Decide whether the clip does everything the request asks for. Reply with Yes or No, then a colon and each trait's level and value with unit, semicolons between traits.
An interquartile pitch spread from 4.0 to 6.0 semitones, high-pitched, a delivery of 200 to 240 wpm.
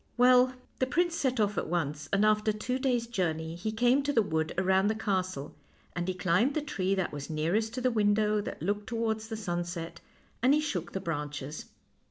Yes: wide, 5.5 semitones; high, 205 Hz; fast, 205 wpm